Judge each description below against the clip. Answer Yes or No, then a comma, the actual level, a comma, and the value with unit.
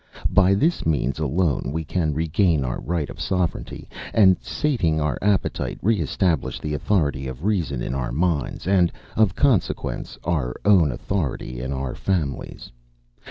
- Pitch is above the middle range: No, very low, 80 Hz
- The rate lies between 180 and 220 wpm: No, average, 150 wpm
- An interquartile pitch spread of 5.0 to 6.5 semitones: Yes, wide, 5.4 semitones